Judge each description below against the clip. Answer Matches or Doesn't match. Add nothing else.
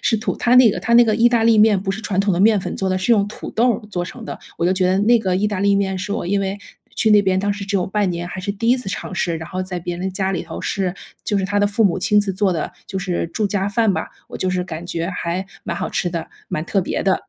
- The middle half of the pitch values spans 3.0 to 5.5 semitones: Doesn't match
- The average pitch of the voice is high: Matches